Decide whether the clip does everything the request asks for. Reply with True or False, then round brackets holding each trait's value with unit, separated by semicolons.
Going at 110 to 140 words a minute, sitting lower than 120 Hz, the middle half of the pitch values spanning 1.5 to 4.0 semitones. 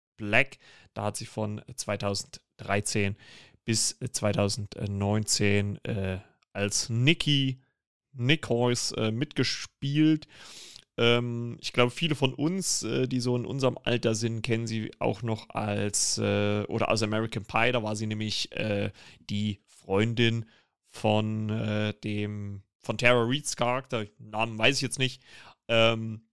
True (130 wpm; 110 Hz; 2.9 semitones)